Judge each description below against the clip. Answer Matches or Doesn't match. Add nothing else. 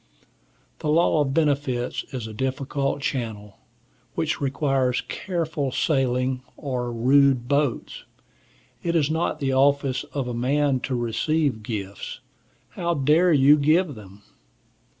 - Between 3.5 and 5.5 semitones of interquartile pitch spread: Doesn't match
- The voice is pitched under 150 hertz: Matches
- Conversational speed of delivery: Doesn't match